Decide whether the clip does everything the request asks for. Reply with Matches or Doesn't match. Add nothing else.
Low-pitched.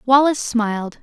Doesn't match